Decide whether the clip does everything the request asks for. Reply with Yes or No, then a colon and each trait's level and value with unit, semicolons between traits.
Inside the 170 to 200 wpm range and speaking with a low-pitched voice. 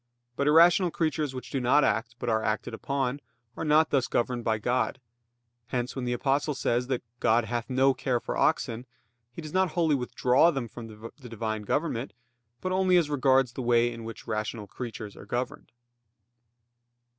Yes: average, 180 wpm; low, 125 Hz